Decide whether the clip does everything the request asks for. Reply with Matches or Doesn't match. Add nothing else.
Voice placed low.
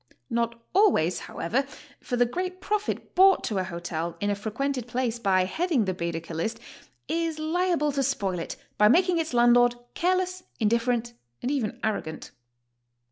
Doesn't match